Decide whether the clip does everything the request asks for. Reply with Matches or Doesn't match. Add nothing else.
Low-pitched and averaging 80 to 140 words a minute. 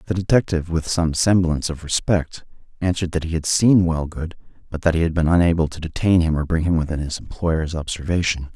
Doesn't match